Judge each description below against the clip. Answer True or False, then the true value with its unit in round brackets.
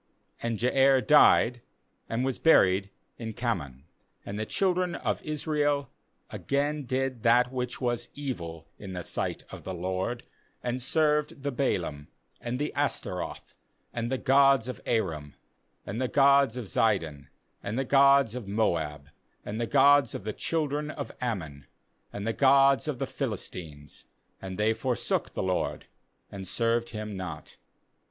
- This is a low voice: True (120 Hz)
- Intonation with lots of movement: True (6.0 semitones)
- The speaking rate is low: False (150 wpm)